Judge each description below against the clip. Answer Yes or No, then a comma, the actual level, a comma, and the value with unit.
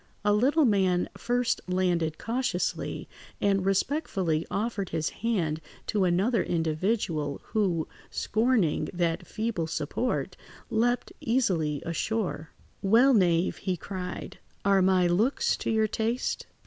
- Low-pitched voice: No, high, 195 Hz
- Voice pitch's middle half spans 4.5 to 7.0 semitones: Yes, average, 4.9 semitones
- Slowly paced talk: Yes, slow, 115 wpm